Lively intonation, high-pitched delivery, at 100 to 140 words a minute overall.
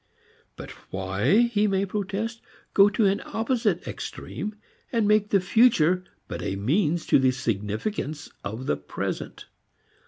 Yes: wide, 8.3 semitones; high, 195 Hz; slow, 135 wpm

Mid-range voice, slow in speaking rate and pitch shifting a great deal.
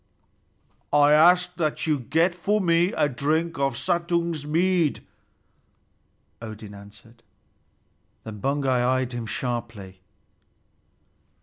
Yes: medium, 145 Hz; slow, 100 wpm; wide, 6.1 semitones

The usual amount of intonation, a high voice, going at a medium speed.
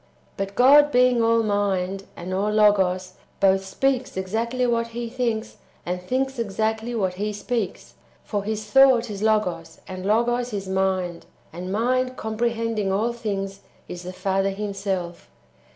Yes: average, 3.5 semitones; high, 210 Hz; average, 150 wpm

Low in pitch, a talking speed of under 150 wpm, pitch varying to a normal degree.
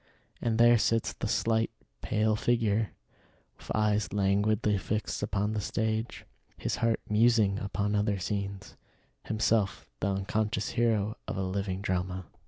No: low, 105 Hz; slow, 135 wpm; narrow, 1.9 semitones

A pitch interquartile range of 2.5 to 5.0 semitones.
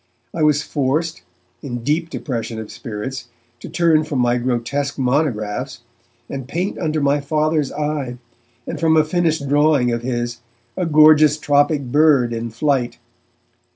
Yes: average, 4.1 semitones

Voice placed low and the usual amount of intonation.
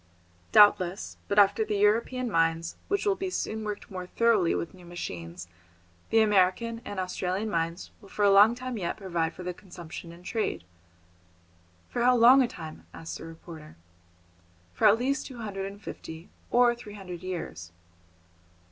No: high, 195 Hz; average, 4.7 semitones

